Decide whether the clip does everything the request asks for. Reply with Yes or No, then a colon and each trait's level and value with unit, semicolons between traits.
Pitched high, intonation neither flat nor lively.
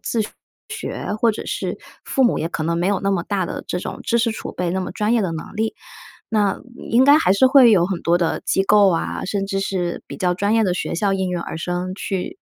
Yes: high, 195 Hz; average, 3.7 semitones